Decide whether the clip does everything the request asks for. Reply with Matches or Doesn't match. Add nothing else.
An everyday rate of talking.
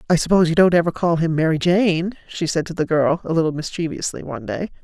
Doesn't match